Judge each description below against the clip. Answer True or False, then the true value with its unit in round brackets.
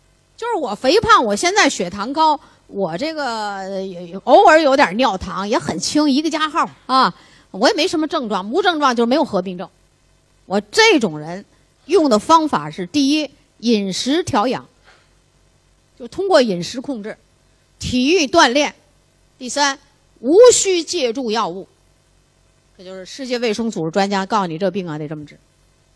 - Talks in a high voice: True (255 Hz)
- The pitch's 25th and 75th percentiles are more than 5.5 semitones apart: True (8.3 semitones)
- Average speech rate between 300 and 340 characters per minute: False (235 characters per minute)